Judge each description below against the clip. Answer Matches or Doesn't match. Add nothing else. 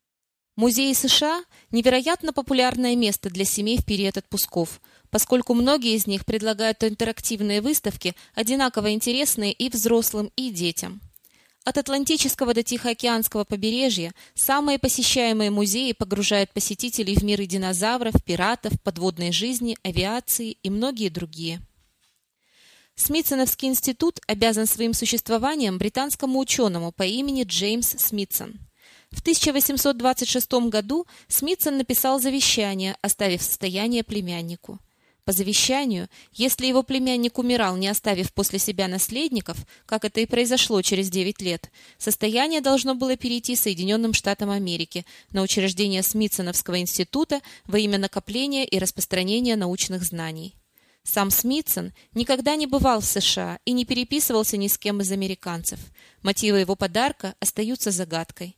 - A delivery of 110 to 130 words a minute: Matches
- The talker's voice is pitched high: Matches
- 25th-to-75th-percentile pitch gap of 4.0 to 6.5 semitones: Matches